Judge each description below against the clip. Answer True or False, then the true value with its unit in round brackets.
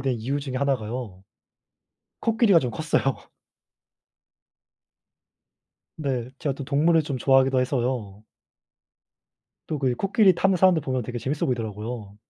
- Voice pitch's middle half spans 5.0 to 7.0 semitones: False (3.7 semitones)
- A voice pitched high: False (130 Hz)